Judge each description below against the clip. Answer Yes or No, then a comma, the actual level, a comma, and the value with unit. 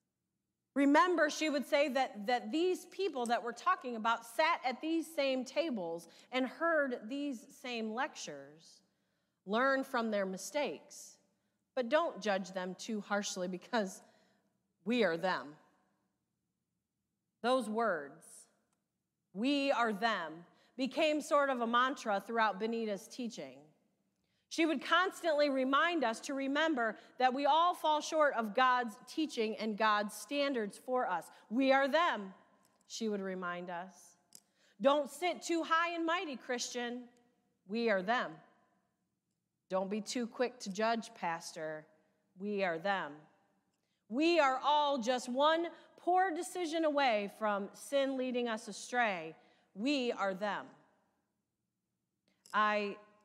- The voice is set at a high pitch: Yes, high, 240 Hz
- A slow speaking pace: Yes, slow, 125 wpm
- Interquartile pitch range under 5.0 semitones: No, wide, 5.6 semitones